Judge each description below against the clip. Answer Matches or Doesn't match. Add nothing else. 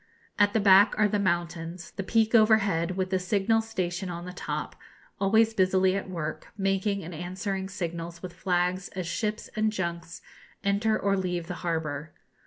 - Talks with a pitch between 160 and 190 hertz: Matches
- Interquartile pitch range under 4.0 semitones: Matches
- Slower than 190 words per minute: Matches